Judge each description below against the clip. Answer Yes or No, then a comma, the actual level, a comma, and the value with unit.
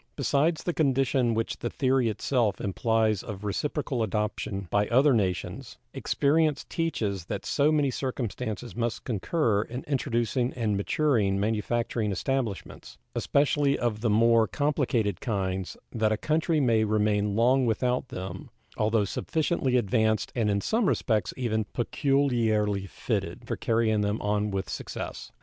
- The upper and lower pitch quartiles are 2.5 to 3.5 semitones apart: No, average, 4.3 semitones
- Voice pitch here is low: Yes, low, 115 Hz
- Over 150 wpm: No, slow, 135 wpm